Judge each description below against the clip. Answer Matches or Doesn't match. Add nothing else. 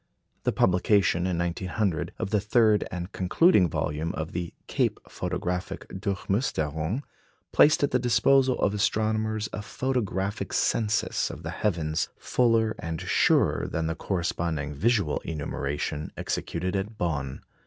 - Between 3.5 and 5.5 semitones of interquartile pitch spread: Matches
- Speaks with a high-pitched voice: Doesn't match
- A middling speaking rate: Doesn't match